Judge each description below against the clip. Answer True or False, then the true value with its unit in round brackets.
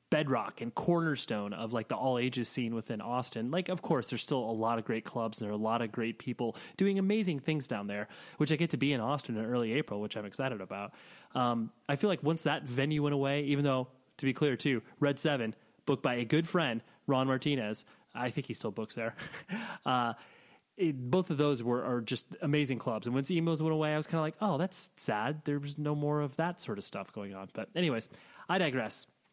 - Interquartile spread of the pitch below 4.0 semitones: False (4.8 semitones)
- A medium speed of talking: False (235 wpm)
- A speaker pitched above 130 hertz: True (140 Hz)